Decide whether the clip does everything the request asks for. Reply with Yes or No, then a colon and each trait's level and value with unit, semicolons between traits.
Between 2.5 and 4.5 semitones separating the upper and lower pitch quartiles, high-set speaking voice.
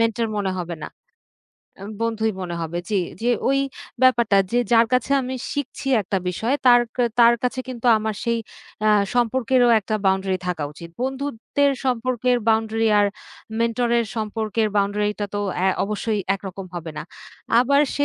Yes: average, 3.3 semitones; high, 225 Hz